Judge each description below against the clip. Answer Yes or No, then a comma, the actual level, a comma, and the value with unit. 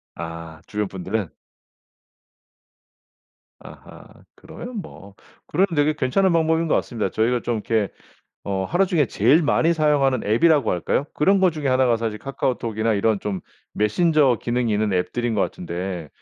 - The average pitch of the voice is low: Yes, low, 120 Hz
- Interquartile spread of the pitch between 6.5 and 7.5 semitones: Yes, wide, 6.8 semitones